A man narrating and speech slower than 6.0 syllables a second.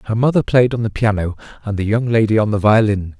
No: male; 6.3 syllables/s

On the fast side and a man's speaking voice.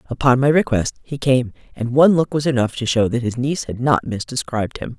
No: fast, 230 wpm; female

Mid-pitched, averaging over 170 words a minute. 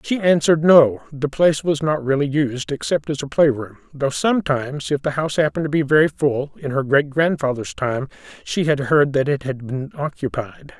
Yes: medium, 145 Hz; average, 200 wpm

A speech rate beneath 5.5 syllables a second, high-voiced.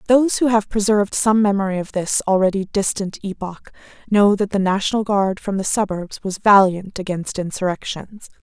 Yes: 5.2 syllables/s; high, 200 Hz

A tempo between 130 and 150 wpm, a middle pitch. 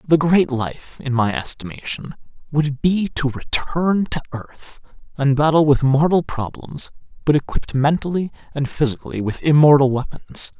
Yes: average, 140 wpm; medium, 145 Hz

